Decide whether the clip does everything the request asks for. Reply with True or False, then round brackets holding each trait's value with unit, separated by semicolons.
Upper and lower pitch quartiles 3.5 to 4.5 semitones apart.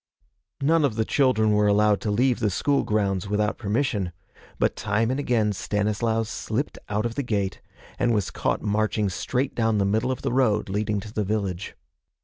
False (2.5 semitones)